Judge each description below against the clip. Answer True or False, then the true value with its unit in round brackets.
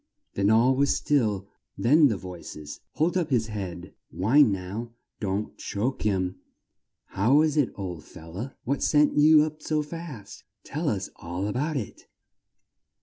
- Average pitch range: False (7.4 semitones)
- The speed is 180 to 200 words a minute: False (155 wpm)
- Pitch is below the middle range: True (115 Hz)